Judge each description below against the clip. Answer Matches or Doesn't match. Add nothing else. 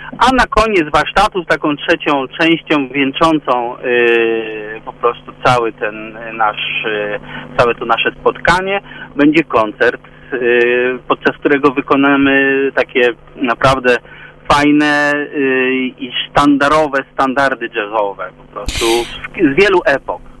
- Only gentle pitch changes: Doesn't match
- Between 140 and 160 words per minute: Doesn't match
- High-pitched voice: Doesn't match